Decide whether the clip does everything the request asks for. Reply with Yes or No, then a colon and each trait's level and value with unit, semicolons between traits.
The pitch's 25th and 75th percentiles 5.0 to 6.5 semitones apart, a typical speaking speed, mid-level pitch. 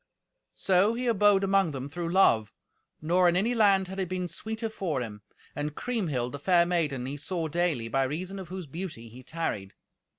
Yes: average, 5.3 semitones; average, 190 wpm; medium, 175 Hz